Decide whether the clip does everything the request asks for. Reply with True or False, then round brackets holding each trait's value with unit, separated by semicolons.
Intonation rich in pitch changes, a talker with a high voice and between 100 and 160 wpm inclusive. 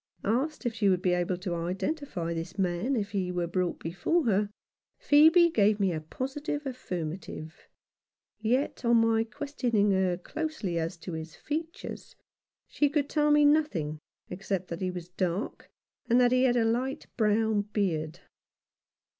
True (6.9 semitones; 205 Hz; 155 wpm)